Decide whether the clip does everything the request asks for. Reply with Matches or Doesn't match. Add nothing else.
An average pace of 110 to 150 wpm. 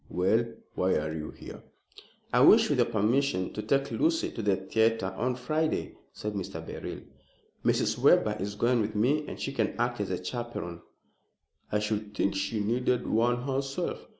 Doesn't match